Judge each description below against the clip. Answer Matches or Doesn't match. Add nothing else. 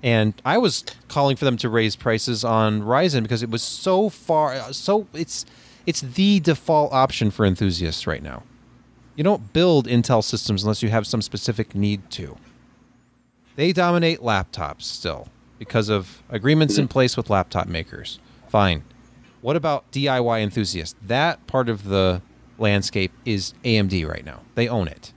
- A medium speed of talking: Matches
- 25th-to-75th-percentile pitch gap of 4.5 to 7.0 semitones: Matches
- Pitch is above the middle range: Doesn't match